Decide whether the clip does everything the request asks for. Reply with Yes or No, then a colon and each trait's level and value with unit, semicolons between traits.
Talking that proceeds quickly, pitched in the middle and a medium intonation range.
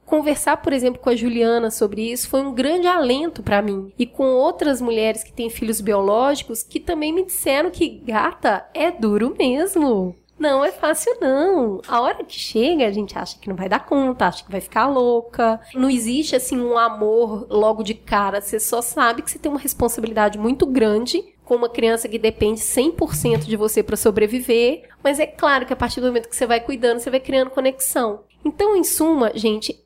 No: fast, 200 wpm; high, 245 Hz; average, 4.6 semitones